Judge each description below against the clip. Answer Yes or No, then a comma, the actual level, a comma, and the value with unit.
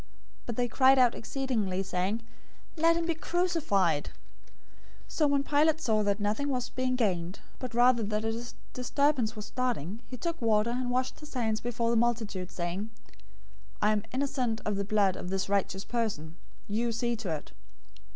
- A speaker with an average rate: Yes, average, 170 wpm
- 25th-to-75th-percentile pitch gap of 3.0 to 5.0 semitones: Yes, average, 3.9 semitones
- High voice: Yes, high, 230 Hz